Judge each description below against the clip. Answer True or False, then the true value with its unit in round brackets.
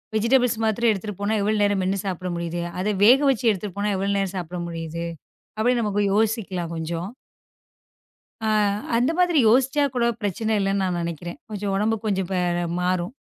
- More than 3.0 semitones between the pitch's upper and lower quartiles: True (3.5 semitones)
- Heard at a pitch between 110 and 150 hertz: False (200 Hz)